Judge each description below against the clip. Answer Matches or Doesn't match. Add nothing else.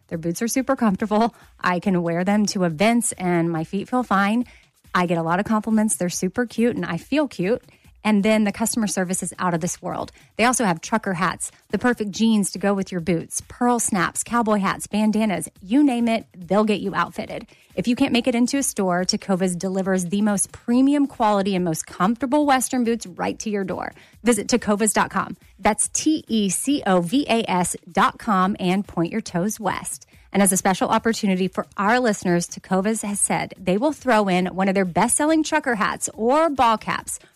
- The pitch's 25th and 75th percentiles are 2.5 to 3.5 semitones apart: Doesn't match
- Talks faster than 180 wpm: Matches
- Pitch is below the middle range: Doesn't match